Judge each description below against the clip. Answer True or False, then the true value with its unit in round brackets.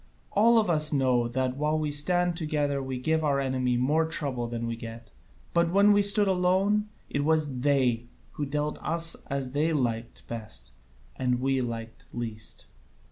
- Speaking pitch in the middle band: True (145 Hz)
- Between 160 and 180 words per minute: True (175 wpm)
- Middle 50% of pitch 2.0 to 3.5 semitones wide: False (4.6 semitones)